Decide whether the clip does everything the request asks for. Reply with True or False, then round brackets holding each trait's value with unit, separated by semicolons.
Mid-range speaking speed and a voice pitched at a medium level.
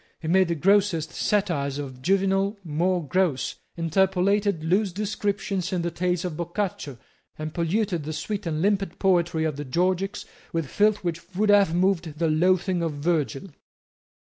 True (155 wpm; 180 Hz)